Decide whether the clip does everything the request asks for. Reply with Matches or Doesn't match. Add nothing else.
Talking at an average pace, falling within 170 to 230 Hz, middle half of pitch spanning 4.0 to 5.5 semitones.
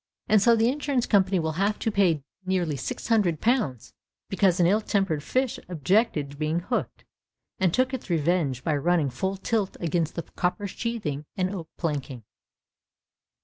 Matches